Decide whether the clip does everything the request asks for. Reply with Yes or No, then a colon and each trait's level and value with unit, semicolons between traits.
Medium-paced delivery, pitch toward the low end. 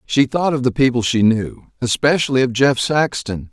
Yes: average, 190 wpm; low, 130 Hz